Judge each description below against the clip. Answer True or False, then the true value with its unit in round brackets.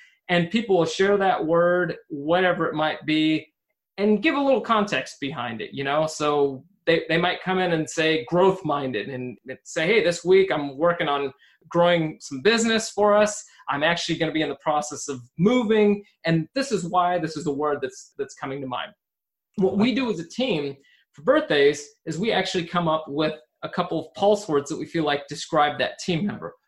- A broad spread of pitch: False (4.9 semitones)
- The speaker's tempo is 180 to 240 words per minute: True (200 wpm)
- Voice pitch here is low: False (165 Hz)